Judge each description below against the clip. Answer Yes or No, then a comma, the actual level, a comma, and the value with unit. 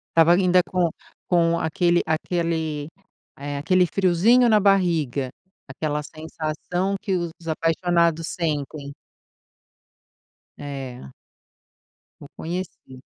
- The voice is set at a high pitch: No, medium, 165 Hz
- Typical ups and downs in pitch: Yes, average, 3.2 semitones